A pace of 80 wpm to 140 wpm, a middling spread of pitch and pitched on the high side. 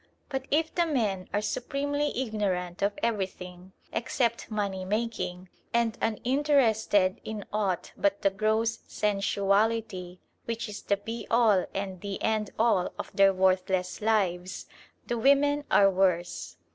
Yes: slow, 135 wpm; average, 3.4 semitones; high, 210 Hz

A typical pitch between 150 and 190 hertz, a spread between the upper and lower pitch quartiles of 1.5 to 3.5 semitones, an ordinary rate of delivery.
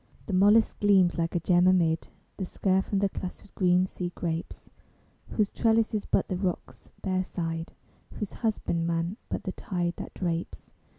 Yes: medium, 185 Hz; narrow, 2.6 semitones; average, 165 wpm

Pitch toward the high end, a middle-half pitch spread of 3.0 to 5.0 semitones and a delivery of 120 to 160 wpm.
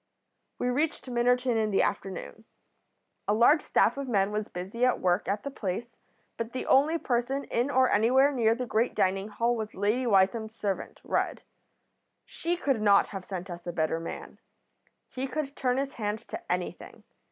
No: high, 230 Hz; average, 4.2 semitones; average, 175 wpm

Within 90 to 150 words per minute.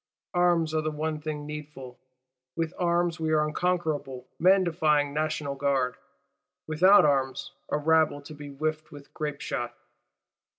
Yes: average, 140 wpm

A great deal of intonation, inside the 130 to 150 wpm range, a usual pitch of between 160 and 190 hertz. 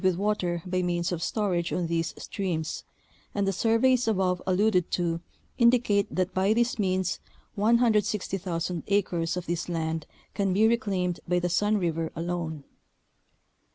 No: average, 3.3 semitones; average, 145 wpm; medium, 185 Hz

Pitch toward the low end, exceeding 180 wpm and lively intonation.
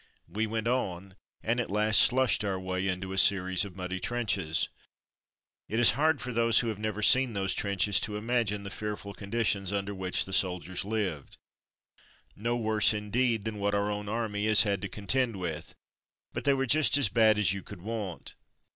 No: low, 105 Hz; average, 190 wpm; average, 3.0 semitones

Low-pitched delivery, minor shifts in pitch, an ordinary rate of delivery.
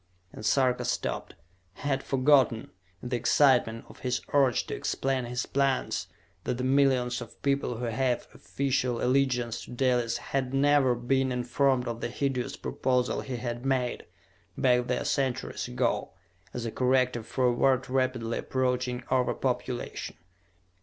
Yes: low, 125 Hz; narrow, 1.6 semitones; average, 150 wpm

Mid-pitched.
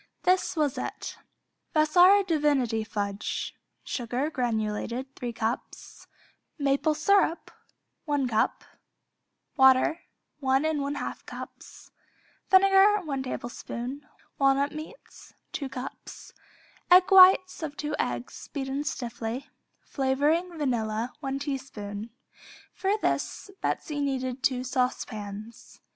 No: very high, 275 Hz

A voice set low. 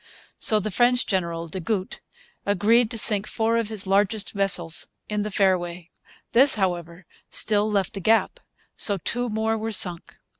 No: high, 205 Hz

